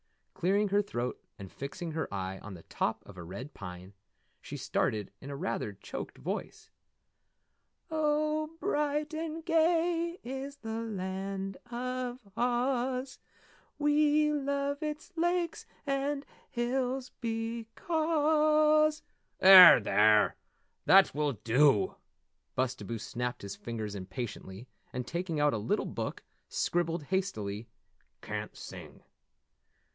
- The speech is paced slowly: Yes, slow, 115 wpm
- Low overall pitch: No, high, 225 Hz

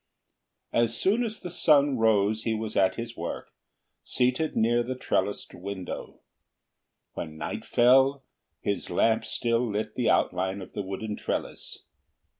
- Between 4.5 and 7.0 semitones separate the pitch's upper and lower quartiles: No, average, 3.8 semitones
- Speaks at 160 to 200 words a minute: No, average, 140 wpm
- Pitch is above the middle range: No, low, 115 Hz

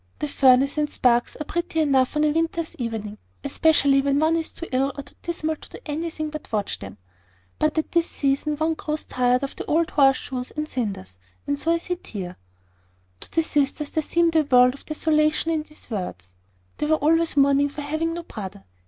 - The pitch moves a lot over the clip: No, average, 3.7 semitones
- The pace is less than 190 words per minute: No, fast, 205 wpm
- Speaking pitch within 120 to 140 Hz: No, very high, 295 Hz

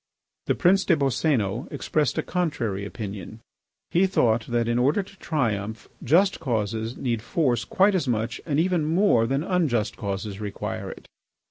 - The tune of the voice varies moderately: No, wide, 7.1 semitones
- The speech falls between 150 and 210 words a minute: Yes, average, 155 wpm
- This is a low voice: Yes, low, 125 Hz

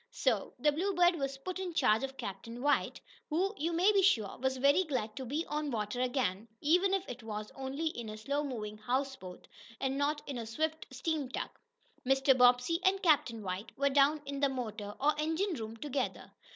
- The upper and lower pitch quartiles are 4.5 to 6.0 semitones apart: Yes, average, 4.8 semitones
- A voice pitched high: Yes, very high, 270 Hz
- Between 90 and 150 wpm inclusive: No, average, 200 wpm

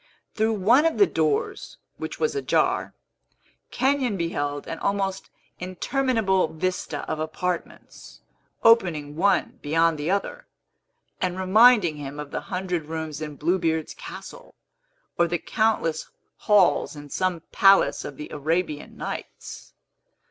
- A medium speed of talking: No, slow, 125 wpm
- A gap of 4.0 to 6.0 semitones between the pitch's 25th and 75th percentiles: Yes, average, 4.9 semitones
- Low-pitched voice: No, medium, 180 Hz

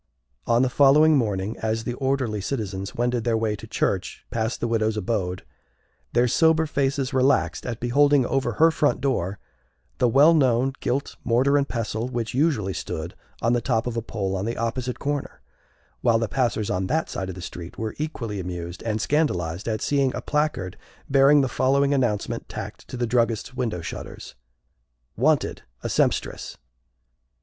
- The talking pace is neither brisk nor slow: Yes, average, 170 wpm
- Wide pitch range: No, average, 4.2 semitones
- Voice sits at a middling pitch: No, low, 120 Hz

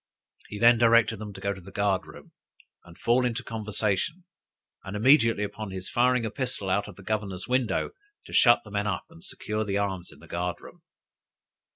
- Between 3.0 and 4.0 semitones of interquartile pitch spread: Yes, average, 3.3 semitones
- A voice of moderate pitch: No, low, 105 Hz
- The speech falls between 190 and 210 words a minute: Yes, average, 200 wpm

